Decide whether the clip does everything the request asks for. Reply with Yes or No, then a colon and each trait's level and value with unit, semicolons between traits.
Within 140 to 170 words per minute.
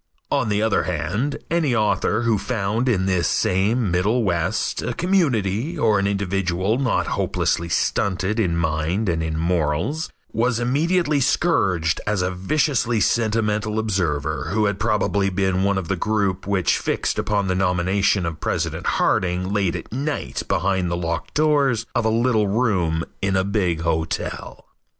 Yes: average, 155 wpm